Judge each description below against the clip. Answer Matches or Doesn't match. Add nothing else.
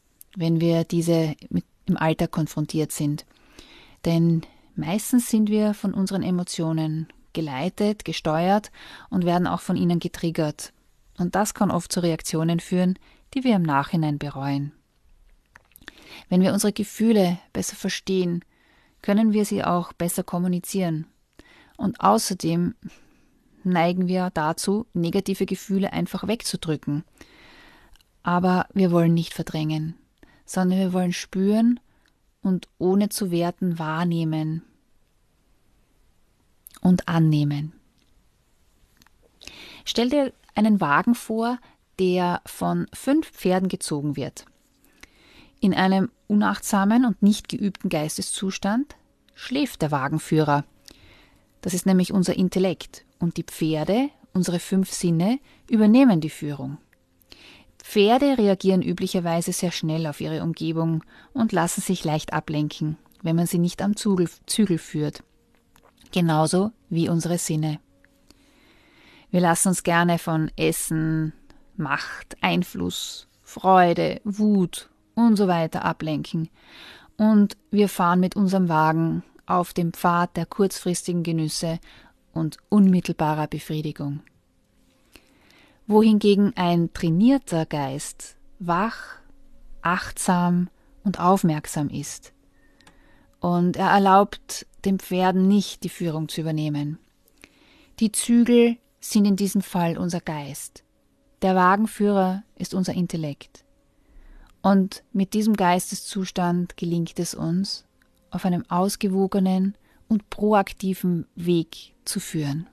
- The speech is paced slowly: Matches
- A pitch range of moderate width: Matches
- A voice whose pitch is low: Doesn't match